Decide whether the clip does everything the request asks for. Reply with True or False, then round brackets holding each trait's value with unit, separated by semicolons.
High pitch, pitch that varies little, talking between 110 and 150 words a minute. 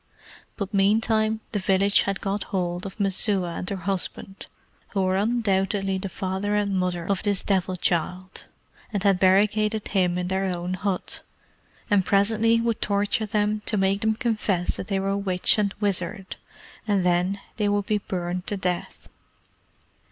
False (195 Hz; 1.9 semitones; 160 wpm)